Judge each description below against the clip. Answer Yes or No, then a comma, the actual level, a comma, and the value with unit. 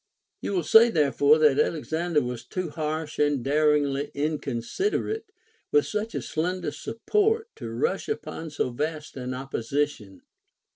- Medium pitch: Yes, medium, 155 Hz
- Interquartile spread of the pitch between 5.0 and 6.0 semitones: No, average, 4.5 semitones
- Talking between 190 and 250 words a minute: No, average, 140 wpm